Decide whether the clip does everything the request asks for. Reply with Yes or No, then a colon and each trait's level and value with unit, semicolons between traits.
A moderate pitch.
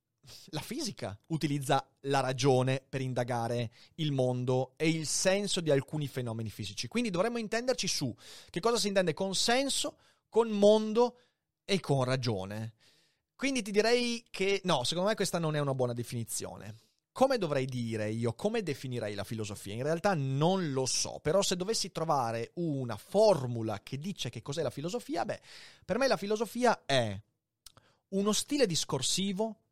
Yes: medium, 155 Hz